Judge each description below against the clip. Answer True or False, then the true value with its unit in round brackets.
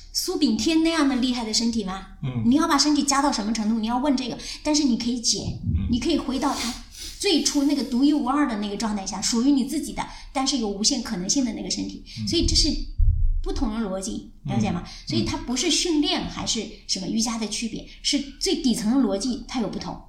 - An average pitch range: True (4.3 semitones)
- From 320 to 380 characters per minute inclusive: True (335 characters per minute)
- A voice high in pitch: True (255 Hz)